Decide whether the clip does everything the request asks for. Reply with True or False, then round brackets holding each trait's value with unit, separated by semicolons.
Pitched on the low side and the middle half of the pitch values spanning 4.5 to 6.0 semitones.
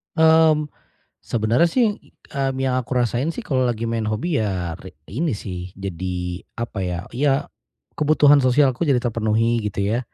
True (120 Hz; 5.3 semitones)